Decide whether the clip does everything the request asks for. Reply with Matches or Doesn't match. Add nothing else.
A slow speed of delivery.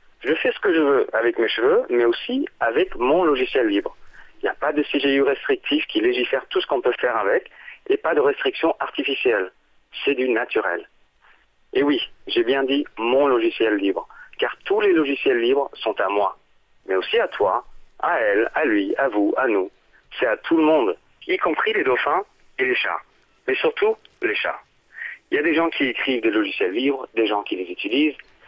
Doesn't match